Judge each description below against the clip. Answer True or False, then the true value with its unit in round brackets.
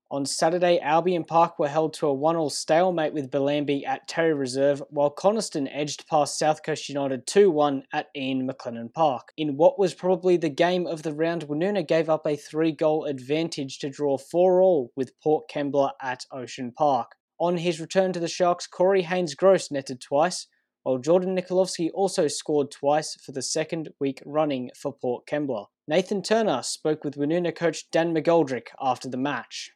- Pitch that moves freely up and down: False (3.4 semitones)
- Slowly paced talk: False (175 wpm)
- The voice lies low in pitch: False (155 Hz)